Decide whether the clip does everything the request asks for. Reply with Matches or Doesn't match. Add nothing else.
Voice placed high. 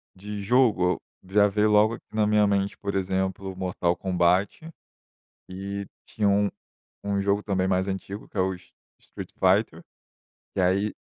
Doesn't match